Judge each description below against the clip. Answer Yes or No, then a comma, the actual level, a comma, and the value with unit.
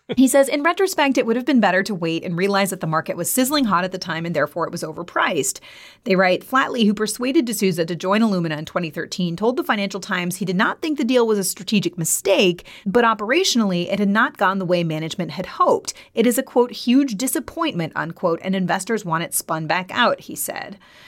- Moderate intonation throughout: No, wide, 6.4 semitones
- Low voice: No, high, 200 Hz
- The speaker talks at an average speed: No, fast, 225 wpm